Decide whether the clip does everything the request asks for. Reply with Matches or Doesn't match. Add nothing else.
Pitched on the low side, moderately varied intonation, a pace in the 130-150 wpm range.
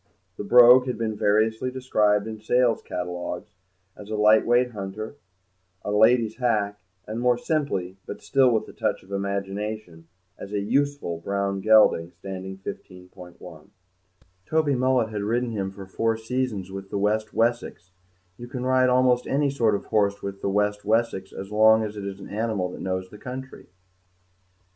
Doesn't match